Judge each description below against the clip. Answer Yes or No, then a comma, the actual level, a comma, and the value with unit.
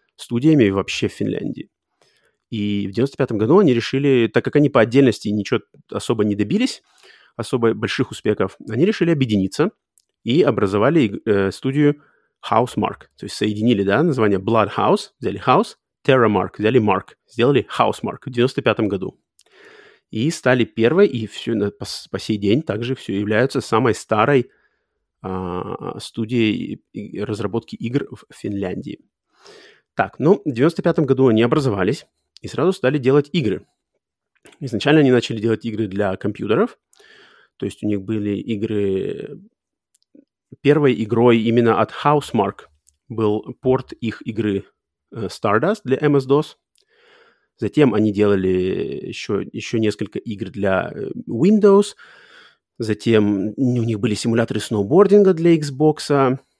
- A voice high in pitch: No, low, 115 Hz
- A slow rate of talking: No, average, 130 wpm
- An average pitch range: Yes, average, 5.0 semitones